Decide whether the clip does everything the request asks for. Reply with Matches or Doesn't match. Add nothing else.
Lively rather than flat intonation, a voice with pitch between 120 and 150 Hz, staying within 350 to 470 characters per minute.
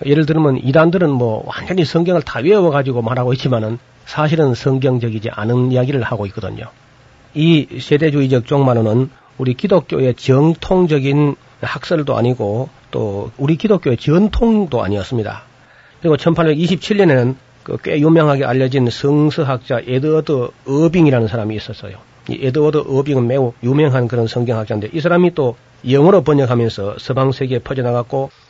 Doesn't match